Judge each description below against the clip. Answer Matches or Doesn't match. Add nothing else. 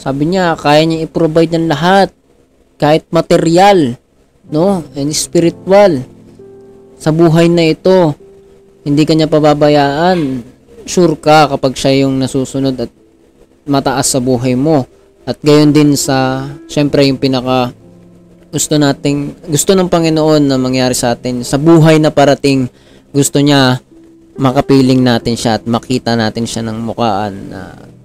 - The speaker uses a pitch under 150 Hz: Matches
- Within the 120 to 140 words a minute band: Matches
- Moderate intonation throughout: Matches